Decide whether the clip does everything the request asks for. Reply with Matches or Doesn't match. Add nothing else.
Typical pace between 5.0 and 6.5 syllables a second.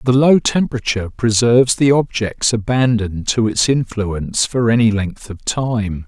Doesn't match